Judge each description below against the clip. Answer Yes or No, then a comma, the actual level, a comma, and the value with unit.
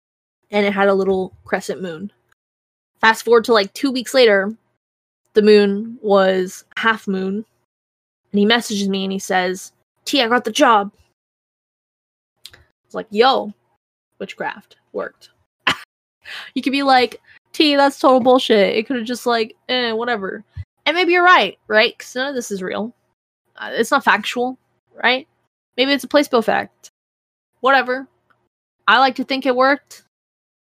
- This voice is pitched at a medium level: No, high, 235 Hz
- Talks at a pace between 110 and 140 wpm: No, average, 155 wpm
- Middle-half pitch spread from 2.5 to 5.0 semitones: Yes, average, 4.5 semitones